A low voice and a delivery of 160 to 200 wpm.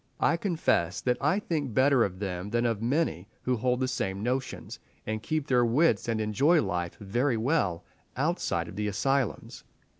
Yes: low, 120 Hz; average, 175 wpm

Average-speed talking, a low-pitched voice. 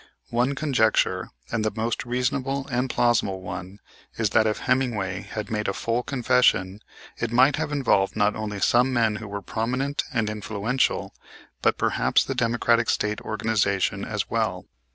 Yes: average, 155 wpm; low, 115 Hz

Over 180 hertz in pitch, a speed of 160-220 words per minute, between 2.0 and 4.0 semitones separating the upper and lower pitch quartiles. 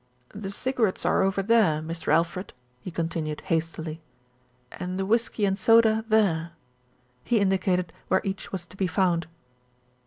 No: high, 190 Hz; average, 150 wpm; average, 3.6 semitones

